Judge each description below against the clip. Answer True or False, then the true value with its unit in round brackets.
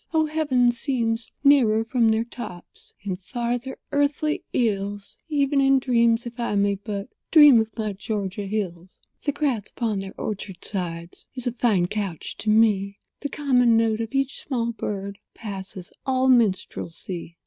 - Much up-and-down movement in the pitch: False (4.2 semitones)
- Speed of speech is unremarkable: True (155 wpm)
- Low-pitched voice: False (225 Hz)